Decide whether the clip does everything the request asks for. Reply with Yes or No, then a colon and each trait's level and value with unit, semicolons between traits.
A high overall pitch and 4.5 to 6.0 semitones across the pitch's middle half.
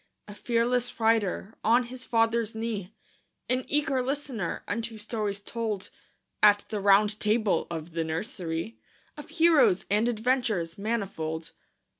No: high, 220 Hz; average, 3.2 semitones